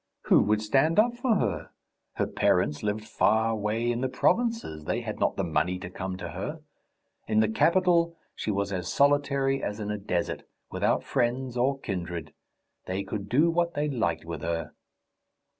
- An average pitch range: No, wide, 7.0 semitones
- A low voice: Yes, low, 110 Hz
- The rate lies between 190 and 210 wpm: No, average, 175 wpm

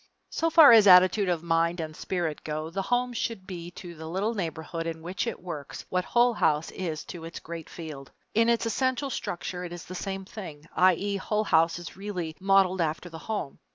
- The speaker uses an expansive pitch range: No, average, 3.6 semitones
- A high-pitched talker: No, medium, 180 Hz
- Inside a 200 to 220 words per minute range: Yes, fast, 205 wpm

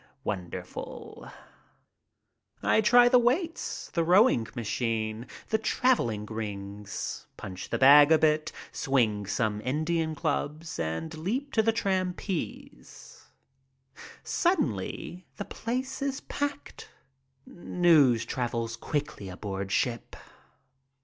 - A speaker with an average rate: No, slow, 100 wpm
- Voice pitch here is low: No, medium, 150 Hz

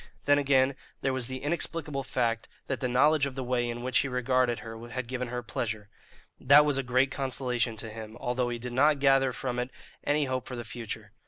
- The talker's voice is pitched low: Yes, low, 125 Hz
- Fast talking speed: Yes, fast, 220 wpm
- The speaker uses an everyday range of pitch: No, narrow, 2.2 semitones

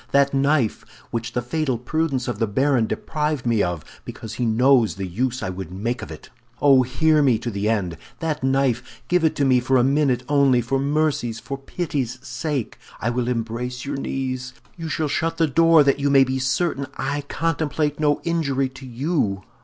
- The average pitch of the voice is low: Yes, low, 130 Hz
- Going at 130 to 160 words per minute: No, average, 195 wpm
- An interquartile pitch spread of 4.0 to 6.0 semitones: No, average, 3.4 semitones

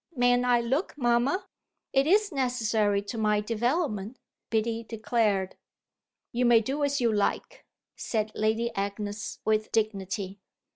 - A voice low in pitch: No, high, 230 Hz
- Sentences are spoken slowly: Yes, slow, 130 wpm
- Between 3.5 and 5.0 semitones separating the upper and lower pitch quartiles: No, average, 2.8 semitones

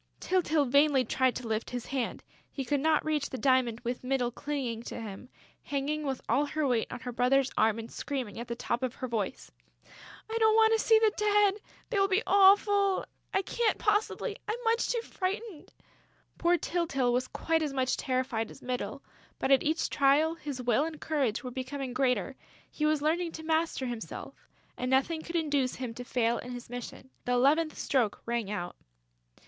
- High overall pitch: Yes, very high, 275 Hz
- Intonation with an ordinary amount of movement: Yes, average, 4.9 semitones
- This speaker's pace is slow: No, average, 195 wpm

